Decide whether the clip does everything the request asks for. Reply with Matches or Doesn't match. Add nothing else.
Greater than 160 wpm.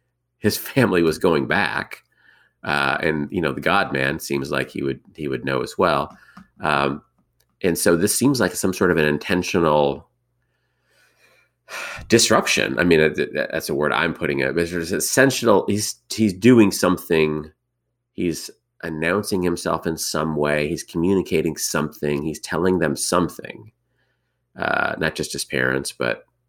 Doesn't match